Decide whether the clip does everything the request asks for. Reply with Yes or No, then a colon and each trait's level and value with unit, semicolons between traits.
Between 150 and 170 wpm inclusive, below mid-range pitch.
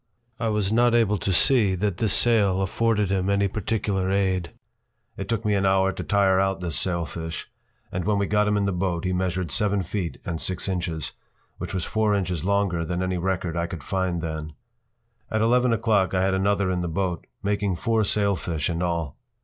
No: average, 200 wpm; very low, 95 Hz